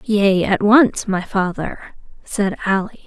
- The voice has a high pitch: Yes, high, 200 Hz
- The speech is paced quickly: No, slow, 135 wpm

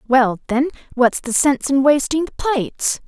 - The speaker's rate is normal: Yes, average, 175 wpm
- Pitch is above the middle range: Yes, very high, 270 Hz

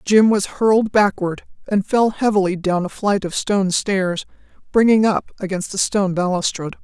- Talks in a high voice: Yes, high, 200 Hz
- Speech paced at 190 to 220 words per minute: No, average, 165 wpm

